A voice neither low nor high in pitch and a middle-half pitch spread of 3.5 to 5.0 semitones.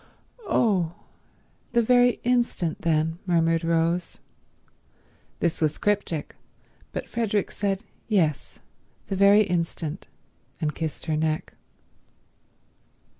Yes: medium, 175 Hz; average, 4.2 semitones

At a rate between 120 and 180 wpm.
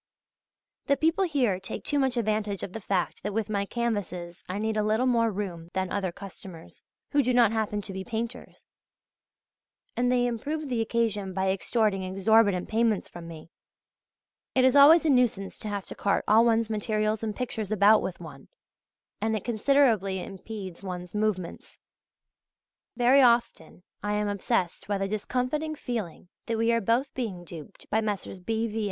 Yes: average, 170 wpm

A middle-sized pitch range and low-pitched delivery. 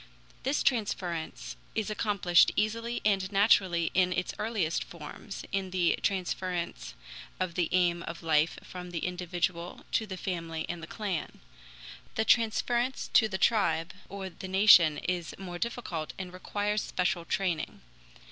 No: average, 3.3 semitones; medium, 185 Hz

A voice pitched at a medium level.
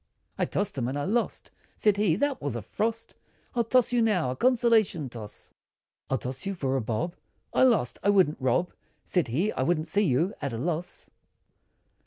Yes: medium, 175 Hz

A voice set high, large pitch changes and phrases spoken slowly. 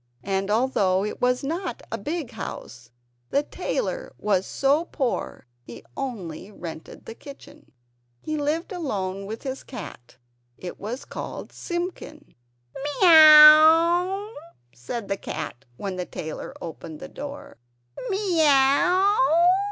Yes: very high, 270 Hz; wide, 8.5 semitones; slow, 120 wpm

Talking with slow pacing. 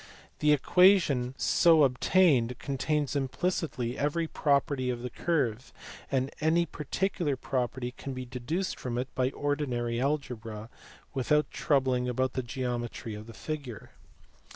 Yes: slow, 130 wpm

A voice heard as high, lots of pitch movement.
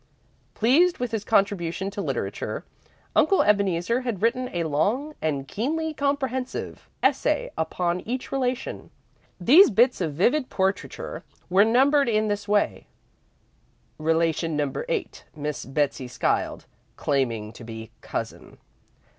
Yes: high, 205 Hz; wide, 7.9 semitones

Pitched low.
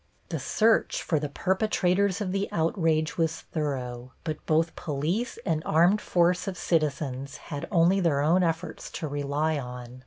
No: medium, 160 Hz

